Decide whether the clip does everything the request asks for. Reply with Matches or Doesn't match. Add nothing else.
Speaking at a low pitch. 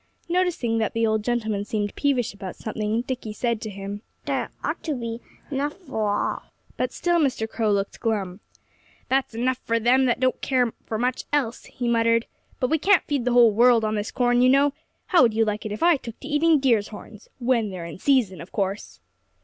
Doesn't match